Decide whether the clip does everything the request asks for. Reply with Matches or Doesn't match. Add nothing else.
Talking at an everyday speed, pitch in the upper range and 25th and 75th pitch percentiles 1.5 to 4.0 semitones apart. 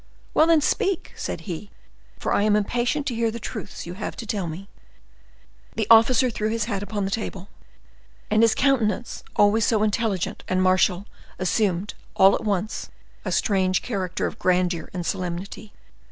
Matches